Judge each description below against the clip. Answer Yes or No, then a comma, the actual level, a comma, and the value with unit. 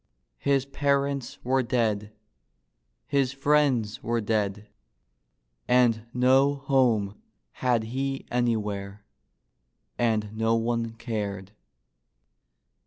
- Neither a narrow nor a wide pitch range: Yes, average, 3.8 semitones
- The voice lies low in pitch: Yes, low, 120 Hz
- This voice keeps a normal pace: No, slow, 85 wpm